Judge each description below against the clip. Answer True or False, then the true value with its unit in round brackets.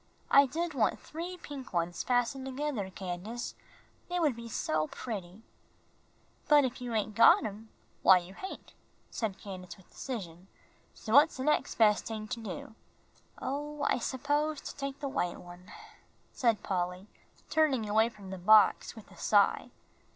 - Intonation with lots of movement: True (6.4 semitones)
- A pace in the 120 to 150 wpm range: False (160 wpm)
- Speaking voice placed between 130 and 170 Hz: False (225 Hz)